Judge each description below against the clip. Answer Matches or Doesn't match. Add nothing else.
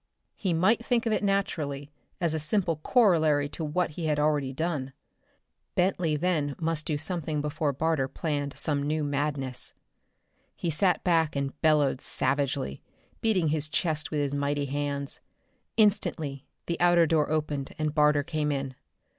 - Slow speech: Doesn't match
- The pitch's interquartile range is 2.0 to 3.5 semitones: Matches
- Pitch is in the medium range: Matches